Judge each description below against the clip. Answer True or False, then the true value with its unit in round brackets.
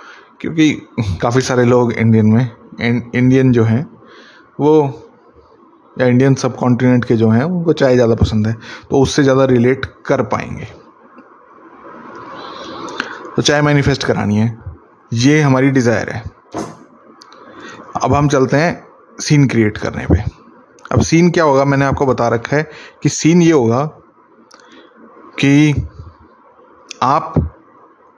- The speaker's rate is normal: True (130 wpm)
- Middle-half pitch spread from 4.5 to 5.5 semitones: False (3.5 semitones)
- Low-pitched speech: True (130 Hz)